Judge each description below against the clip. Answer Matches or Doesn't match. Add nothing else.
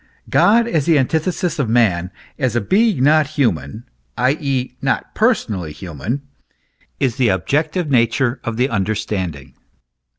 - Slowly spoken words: Matches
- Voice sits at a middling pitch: Doesn't match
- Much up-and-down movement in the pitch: Matches